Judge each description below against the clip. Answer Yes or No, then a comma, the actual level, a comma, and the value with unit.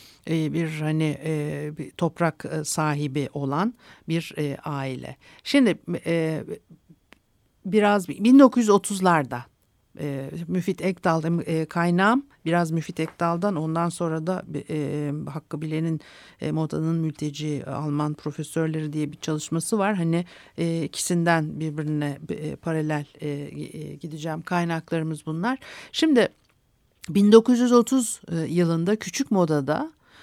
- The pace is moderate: Yes, average, 105 wpm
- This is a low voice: No, medium, 165 Hz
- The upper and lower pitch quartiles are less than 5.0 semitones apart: Yes, average, 3.1 semitones